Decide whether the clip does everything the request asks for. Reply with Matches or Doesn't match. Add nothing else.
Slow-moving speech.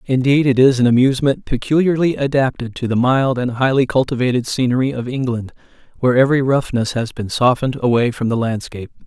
Doesn't match